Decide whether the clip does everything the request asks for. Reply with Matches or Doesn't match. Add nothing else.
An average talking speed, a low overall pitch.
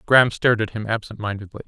Doesn't match